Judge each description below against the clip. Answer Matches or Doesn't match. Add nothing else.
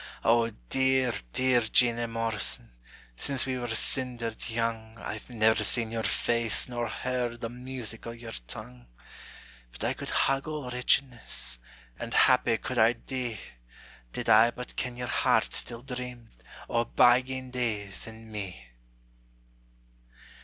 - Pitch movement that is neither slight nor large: Doesn't match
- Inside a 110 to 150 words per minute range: Matches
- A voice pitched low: Matches